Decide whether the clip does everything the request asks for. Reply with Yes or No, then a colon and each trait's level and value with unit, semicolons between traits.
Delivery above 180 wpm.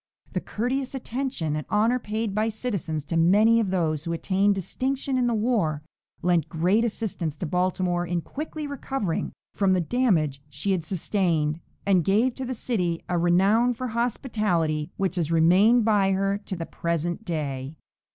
No: average, 165 wpm